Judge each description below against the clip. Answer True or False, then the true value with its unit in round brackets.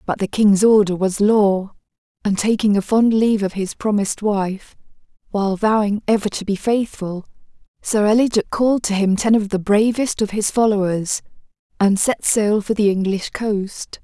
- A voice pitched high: True (205 Hz)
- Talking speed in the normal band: True (170 wpm)